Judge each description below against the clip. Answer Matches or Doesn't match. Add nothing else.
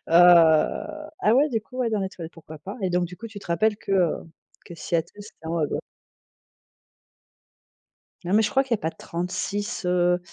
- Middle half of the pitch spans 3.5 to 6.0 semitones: Matches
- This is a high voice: Doesn't match